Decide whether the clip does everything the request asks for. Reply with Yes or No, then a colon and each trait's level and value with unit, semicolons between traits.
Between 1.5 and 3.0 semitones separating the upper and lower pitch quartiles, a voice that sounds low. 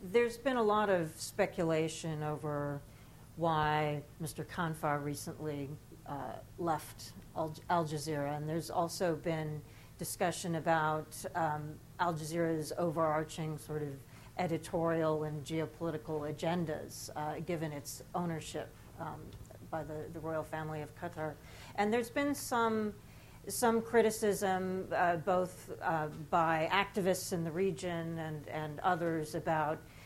No: narrow, 2.5 semitones; medium, 160 Hz